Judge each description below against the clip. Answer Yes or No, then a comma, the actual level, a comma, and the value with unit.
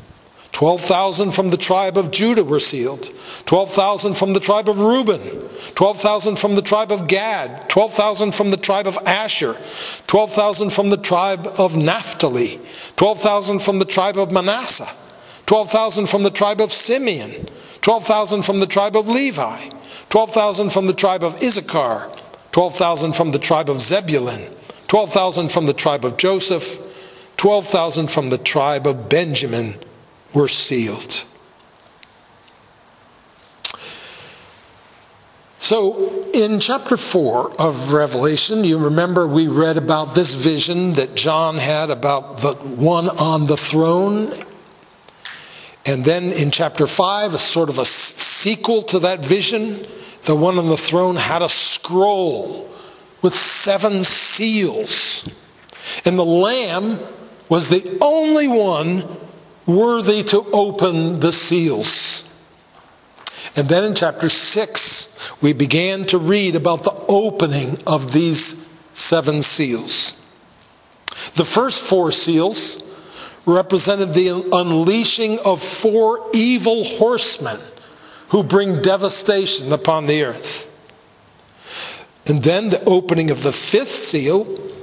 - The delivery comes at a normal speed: No, slow, 125 wpm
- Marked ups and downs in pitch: No, average, 4.5 semitones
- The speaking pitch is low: No, high, 190 Hz